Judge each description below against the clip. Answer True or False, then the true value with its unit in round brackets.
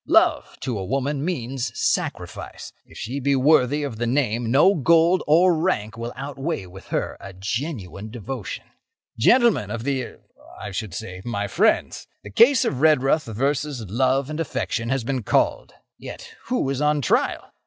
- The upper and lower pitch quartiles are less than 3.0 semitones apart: False (4.7 semitones)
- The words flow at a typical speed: True (160 wpm)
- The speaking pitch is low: True (130 Hz)